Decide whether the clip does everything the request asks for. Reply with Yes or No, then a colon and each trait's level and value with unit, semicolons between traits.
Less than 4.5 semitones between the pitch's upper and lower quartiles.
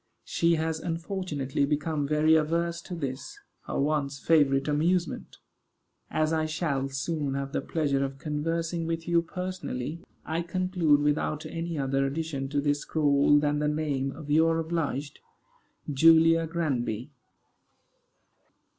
Yes: average, 2.7 semitones